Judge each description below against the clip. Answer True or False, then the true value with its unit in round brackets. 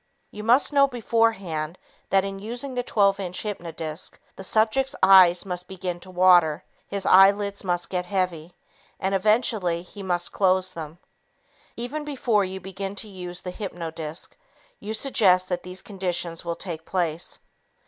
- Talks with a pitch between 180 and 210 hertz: True (190 Hz)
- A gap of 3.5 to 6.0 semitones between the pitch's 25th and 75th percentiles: False (2.7 semitones)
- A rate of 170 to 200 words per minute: False (150 wpm)